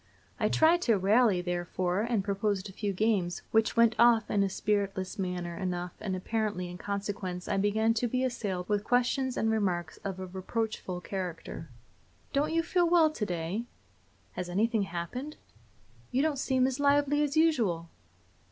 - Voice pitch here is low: No, high, 205 Hz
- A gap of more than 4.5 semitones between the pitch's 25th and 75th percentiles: Yes, average, 5.0 semitones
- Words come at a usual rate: Yes, average, 165 wpm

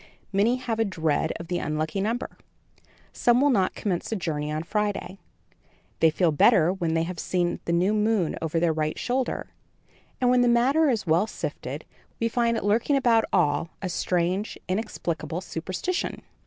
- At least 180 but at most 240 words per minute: No, average, 170 wpm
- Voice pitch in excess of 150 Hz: Yes, high, 190 Hz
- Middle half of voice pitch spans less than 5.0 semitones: No, wide, 5.6 semitones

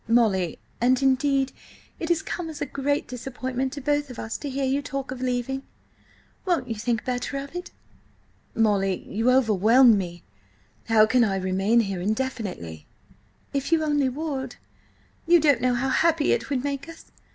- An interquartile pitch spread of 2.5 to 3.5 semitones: No, average, 4.0 semitones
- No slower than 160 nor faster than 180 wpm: Yes, average, 170 wpm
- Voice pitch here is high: Yes, very high, 255 Hz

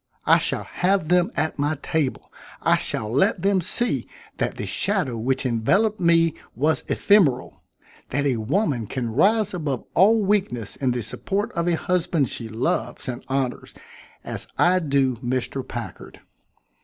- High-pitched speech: No, medium, 150 Hz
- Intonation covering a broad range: Yes, wide, 6.7 semitones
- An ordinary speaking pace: Yes, average, 155 wpm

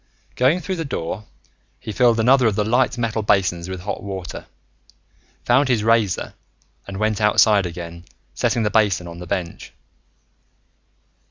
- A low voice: Yes, low, 105 Hz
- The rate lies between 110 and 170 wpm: Yes, average, 150 wpm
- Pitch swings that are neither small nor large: Yes, average, 4.4 semitones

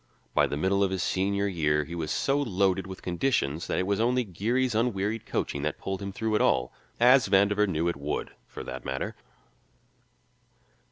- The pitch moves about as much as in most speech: Yes, average, 4.2 semitones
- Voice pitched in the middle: No, very low, 95 Hz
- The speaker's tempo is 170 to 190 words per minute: Yes, average, 185 wpm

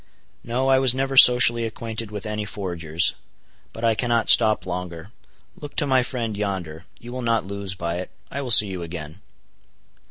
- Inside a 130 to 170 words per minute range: No, average, 180 wpm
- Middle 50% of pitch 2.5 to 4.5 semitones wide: No, average, 4.9 semitones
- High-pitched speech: No, low, 110 Hz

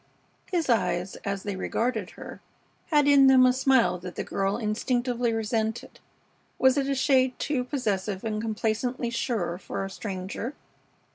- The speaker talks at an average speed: Yes, average, 150 wpm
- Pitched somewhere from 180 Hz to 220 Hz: No, high, 230 Hz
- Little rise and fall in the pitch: No, average, 4.5 semitones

